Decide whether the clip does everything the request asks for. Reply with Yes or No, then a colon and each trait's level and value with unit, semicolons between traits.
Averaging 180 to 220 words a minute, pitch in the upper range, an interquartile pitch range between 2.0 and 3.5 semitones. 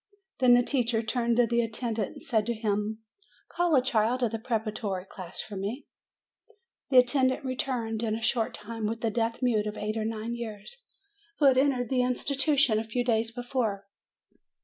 Yes: average, 185 wpm; high, 230 Hz; narrow, 2.5 semitones